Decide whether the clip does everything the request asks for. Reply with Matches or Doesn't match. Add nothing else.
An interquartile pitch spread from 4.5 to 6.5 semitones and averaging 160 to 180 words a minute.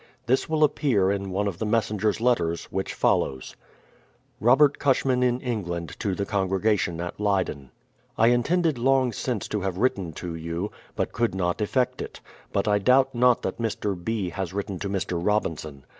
Matches